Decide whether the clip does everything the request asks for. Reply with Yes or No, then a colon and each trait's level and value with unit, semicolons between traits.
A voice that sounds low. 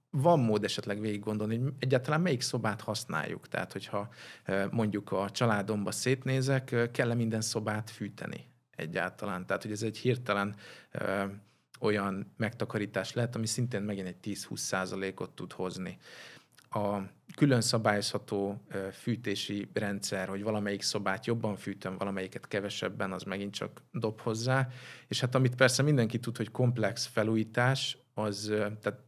Yes: low, 110 Hz